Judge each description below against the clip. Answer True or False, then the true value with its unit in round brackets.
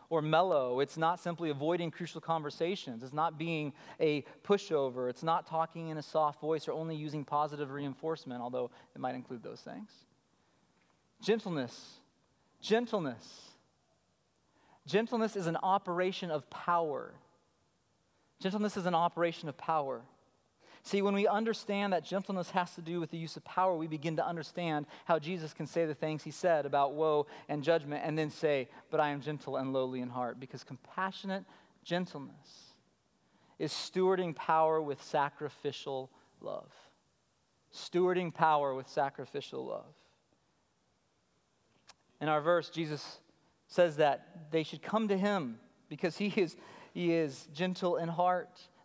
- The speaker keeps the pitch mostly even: False (3.6 semitones)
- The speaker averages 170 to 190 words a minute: False (145 wpm)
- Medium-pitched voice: True (160 Hz)